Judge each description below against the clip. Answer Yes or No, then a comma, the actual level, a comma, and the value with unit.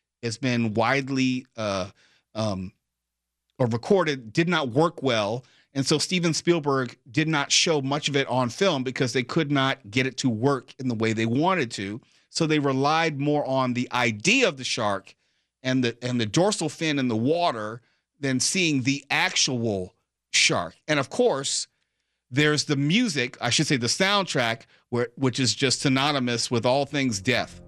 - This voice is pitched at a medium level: No, low, 130 Hz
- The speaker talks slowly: No, average, 175 wpm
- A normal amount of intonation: Yes, average, 4.0 semitones